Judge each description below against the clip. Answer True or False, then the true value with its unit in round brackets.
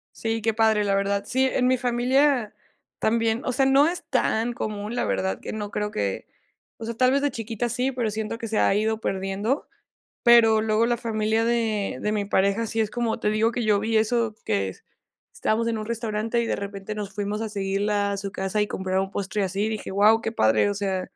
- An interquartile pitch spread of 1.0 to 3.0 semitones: True (2.4 semitones)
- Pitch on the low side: False (220 Hz)